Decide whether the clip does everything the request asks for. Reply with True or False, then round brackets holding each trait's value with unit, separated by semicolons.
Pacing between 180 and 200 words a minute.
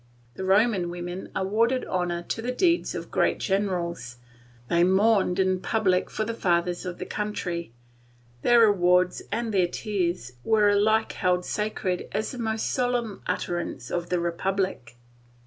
False (145 wpm)